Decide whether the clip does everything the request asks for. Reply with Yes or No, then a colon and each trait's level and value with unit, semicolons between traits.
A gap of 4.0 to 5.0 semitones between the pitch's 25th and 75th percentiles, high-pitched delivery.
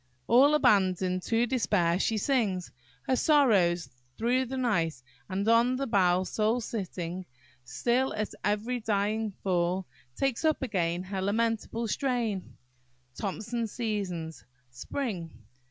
Yes: average, 4.7 semitones; high, 210 Hz